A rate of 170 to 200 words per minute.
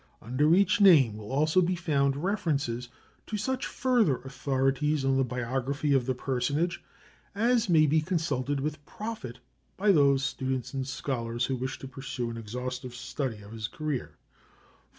No: average, 155 wpm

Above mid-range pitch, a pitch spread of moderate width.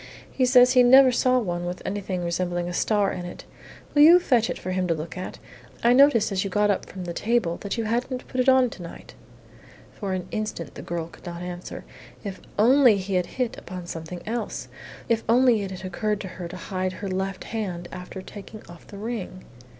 Yes: high, 195 Hz; average, 4.7 semitones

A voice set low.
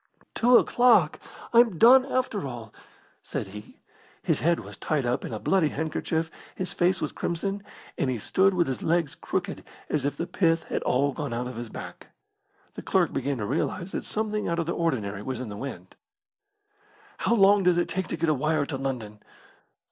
No: medium, 160 Hz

